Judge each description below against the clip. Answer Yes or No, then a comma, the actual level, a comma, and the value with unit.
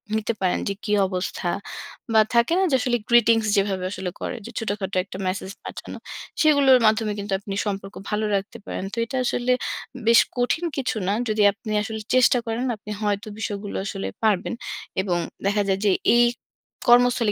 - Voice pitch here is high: Yes, high, 215 Hz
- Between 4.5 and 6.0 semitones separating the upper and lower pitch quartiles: No, average, 3.2 semitones